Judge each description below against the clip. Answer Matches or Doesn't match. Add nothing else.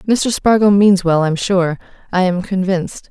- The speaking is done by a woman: Matches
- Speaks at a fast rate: Doesn't match